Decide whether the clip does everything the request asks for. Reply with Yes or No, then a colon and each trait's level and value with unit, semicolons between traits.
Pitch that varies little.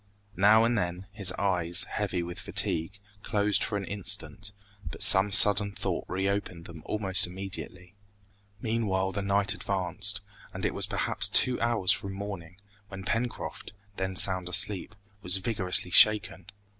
Yes: narrow, 2.1 semitones